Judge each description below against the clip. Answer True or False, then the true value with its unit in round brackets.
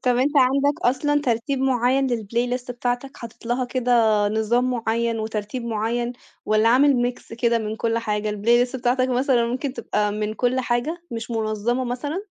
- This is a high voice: True (240 Hz)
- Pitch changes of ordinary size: False (2.1 semitones)